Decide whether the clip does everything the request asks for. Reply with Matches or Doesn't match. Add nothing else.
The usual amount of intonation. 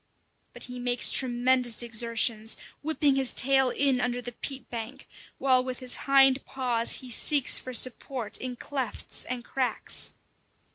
Doesn't match